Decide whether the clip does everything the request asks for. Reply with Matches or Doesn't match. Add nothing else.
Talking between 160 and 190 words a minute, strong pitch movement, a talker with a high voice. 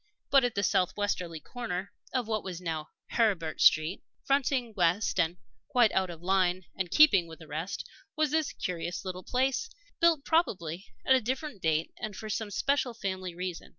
Matches